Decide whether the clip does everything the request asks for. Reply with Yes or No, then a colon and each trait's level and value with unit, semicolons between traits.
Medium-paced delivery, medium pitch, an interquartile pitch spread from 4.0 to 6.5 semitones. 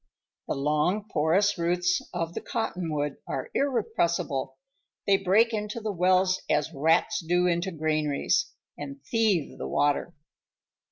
No: slow, 125 wpm; medium, 175 Hz; average, 4.5 semitones